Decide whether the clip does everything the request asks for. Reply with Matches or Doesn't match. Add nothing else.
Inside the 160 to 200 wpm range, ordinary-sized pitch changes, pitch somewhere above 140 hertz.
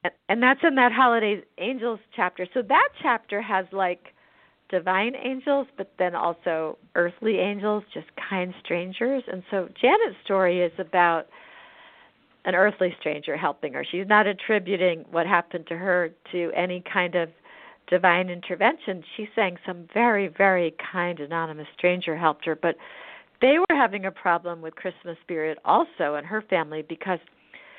Doesn't match